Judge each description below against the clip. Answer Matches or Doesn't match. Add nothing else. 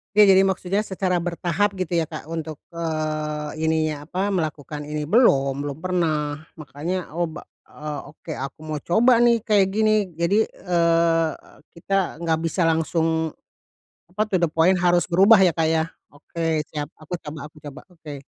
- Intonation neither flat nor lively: Matches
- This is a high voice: Doesn't match